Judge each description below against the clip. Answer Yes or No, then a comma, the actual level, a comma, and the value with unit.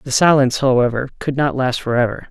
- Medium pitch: No, low, 130 Hz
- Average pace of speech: Yes, average, 180 wpm